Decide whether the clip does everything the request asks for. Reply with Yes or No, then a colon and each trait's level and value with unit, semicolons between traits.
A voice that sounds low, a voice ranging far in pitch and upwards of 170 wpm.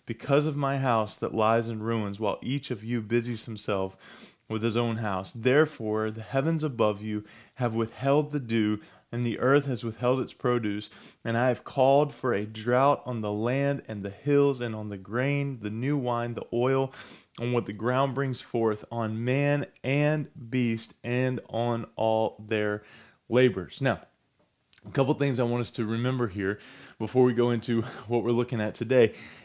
No: low, 120 Hz; average, 2.9 semitones; average, 185 wpm